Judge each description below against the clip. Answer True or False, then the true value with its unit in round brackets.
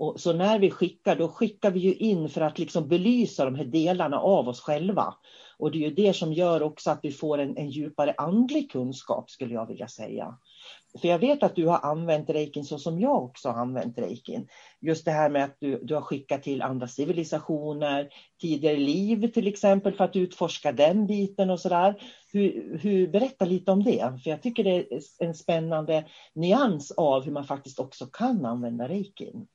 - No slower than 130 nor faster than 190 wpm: False (205 wpm)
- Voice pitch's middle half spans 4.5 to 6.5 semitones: True (4.8 semitones)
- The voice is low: False (165 Hz)